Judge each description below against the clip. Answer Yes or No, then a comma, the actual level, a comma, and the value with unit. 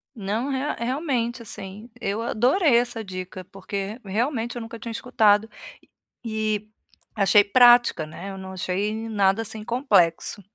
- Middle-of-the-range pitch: No, high, 220 Hz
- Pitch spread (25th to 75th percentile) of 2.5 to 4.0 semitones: Yes, average, 3.4 semitones